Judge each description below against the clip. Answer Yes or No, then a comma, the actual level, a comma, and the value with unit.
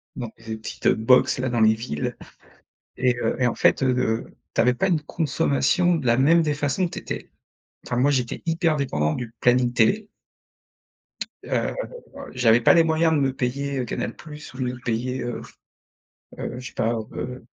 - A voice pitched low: Yes, low, 125 Hz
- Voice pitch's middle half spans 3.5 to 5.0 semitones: Yes, average, 3.8 semitones